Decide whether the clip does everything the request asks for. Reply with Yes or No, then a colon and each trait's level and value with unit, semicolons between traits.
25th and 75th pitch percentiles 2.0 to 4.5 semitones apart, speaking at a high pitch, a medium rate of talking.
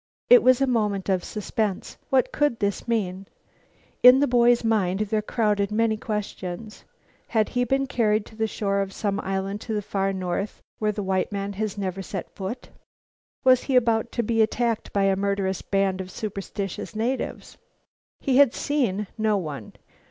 Yes: average, 3.0 semitones; high, 210 Hz; average, 175 wpm